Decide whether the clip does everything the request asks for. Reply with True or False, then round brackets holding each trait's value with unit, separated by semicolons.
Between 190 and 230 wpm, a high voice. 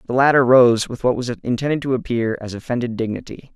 False (205 wpm; 120 Hz)